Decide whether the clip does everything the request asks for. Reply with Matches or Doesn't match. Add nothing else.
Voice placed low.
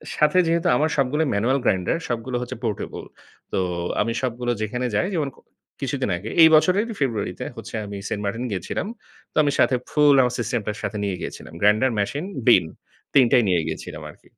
Matches